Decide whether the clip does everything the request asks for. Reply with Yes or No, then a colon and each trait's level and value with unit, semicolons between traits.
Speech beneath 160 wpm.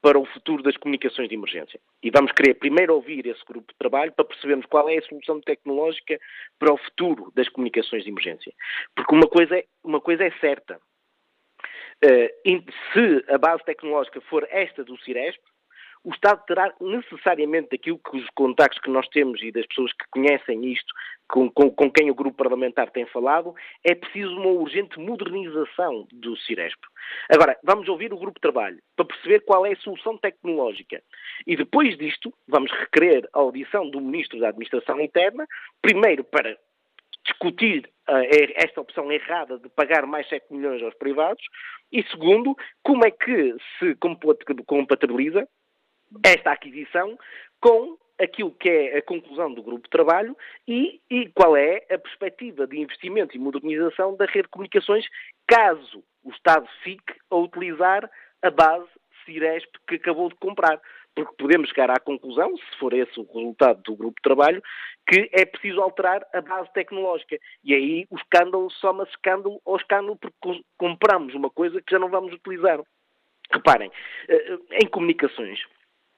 No: average, 165 wpm